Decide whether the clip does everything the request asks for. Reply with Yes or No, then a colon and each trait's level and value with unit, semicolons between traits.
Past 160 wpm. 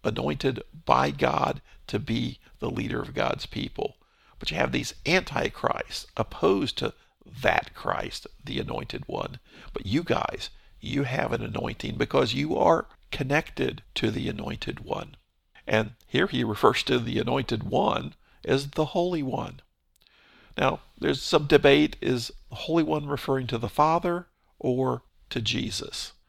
No: average, 145 wpm